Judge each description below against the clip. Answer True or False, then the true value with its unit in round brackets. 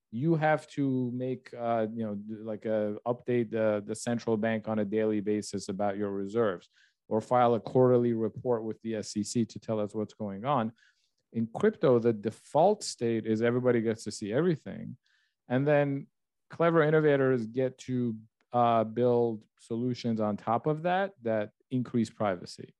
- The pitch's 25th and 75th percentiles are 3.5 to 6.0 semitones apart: False (2.6 semitones)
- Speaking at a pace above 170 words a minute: False (165 wpm)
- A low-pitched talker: True (115 Hz)